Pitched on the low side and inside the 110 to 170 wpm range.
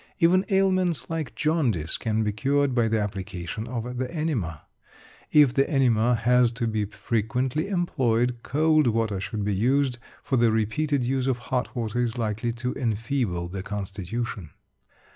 Yes: low, 120 Hz; average, 155 wpm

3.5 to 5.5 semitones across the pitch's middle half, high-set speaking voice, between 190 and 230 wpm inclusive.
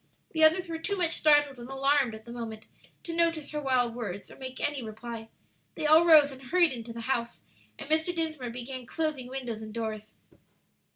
Yes: average, 5.0 semitones; very high, 265 Hz; average, 195 wpm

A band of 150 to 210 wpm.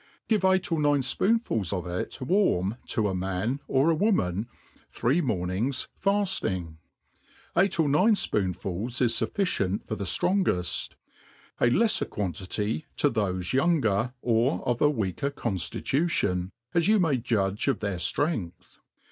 No: average, 140 wpm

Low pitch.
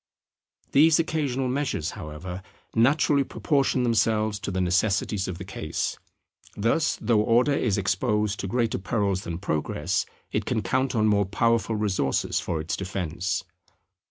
Yes: low, 105 Hz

